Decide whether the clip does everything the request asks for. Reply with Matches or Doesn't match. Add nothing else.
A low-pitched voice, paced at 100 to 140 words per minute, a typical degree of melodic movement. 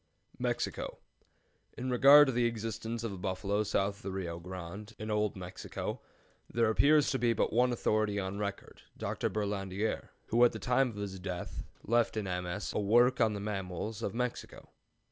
Doesn't match